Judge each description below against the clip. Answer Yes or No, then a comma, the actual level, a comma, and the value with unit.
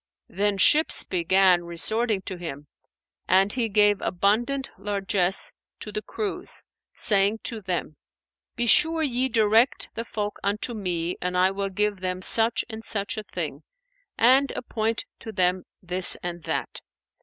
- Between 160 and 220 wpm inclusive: No, average, 145 wpm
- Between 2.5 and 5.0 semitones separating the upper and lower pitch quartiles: Yes, average, 3.7 semitones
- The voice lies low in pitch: No, high, 205 Hz